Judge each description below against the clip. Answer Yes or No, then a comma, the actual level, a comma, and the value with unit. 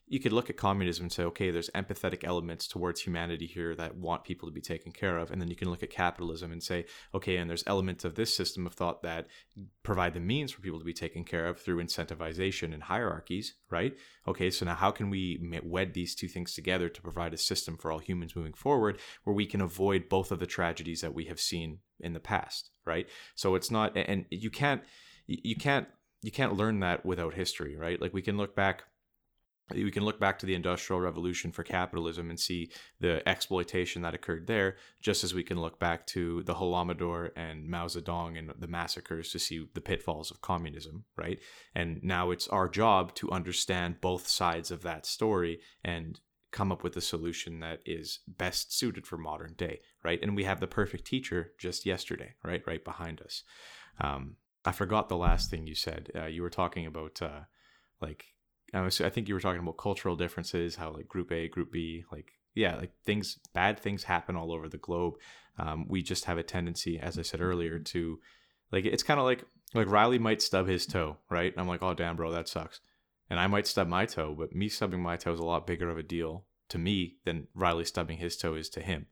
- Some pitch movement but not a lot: No, narrow, 2.1 semitones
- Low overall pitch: Yes, very low, 90 Hz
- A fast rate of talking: Yes, fast, 220 wpm